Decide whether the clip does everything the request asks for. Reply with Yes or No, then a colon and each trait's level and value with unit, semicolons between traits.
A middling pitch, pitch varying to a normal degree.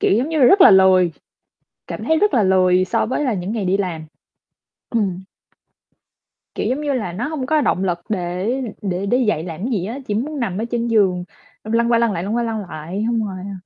No: high, 210 Hz; average, 4.5 semitones